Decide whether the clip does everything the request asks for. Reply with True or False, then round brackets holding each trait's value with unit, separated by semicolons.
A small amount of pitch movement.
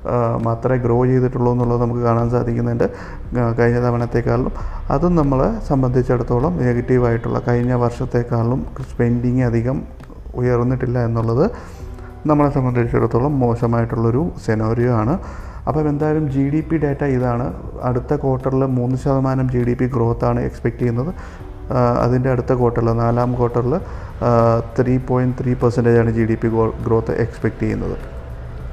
True (1.8 semitones)